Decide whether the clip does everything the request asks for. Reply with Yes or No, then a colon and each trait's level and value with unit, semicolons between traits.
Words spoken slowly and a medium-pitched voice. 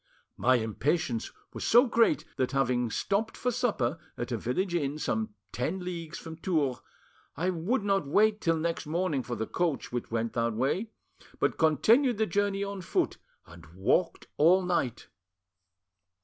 No: average, 165 wpm; medium, 165 Hz